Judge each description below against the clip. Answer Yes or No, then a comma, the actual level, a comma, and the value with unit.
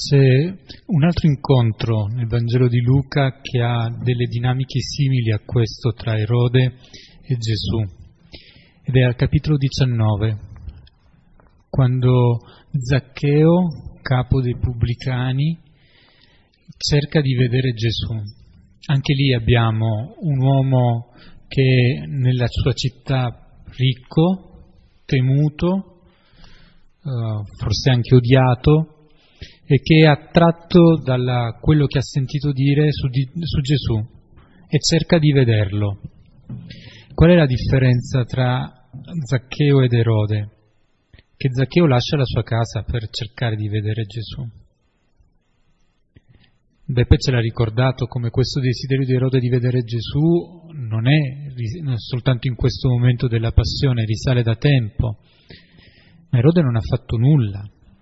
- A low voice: Yes, low, 125 Hz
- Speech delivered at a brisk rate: No, average, 120 wpm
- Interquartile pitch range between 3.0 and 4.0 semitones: Yes, average, 3.4 semitones